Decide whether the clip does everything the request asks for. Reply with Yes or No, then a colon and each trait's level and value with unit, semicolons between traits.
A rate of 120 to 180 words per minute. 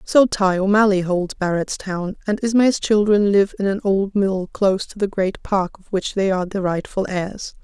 No: average, 195 wpm